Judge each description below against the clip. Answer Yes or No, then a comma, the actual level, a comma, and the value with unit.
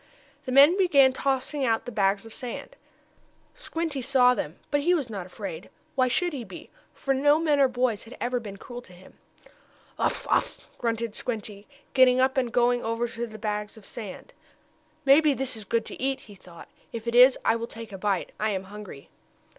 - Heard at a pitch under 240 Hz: No, high, 245 Hz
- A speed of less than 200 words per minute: No, fast, 205 wpm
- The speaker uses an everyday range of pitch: Yes, average, 3.9 semitones